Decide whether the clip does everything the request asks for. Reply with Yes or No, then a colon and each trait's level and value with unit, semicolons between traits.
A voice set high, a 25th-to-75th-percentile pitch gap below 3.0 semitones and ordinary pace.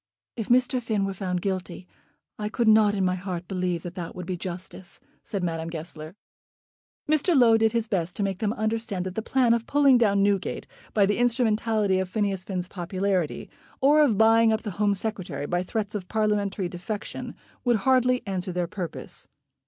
No: high, 200 Hz; average, 3.6 semitones; average, 185 wpm